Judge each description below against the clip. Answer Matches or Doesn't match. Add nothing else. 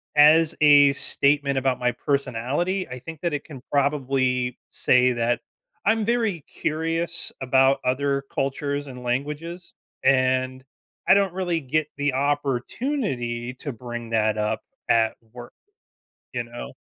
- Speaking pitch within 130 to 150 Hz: Matches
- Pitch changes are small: Doesn't match